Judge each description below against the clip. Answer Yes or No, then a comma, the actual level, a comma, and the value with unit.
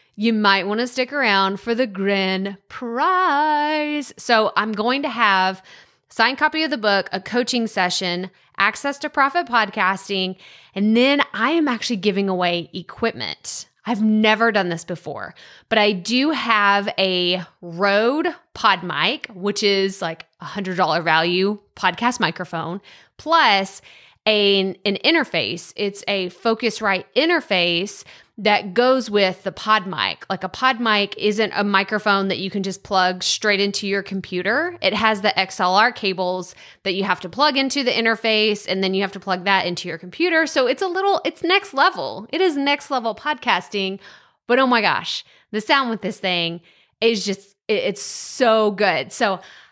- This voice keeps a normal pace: Yes, average, 165 wpm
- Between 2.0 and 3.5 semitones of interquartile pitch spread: No, average, 4.4 semitones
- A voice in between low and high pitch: No, high, 205 Hz